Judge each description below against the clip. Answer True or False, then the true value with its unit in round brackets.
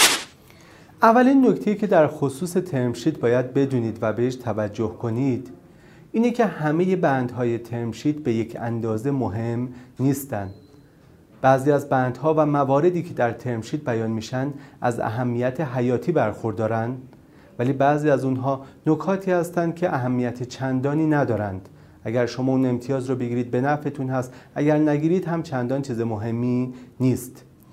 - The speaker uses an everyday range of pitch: True (3.8 semitones)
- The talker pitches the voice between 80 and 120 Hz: False (130 Hz)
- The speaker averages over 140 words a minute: False (135 wpm)